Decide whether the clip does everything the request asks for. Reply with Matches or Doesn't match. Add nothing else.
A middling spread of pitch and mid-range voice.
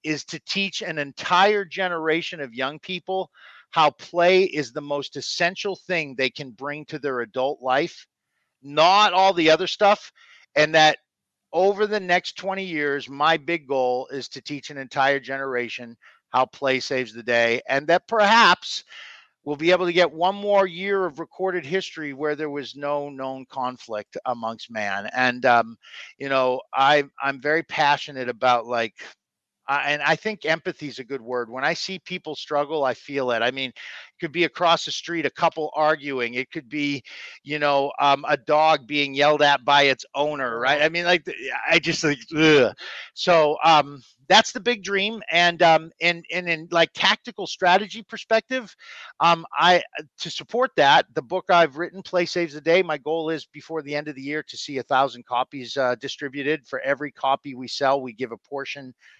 Matches